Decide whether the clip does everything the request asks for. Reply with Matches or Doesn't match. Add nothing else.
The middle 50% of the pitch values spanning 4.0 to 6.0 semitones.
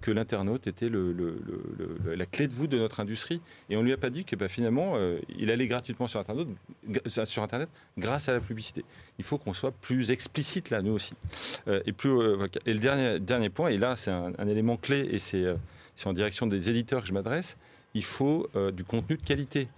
Matches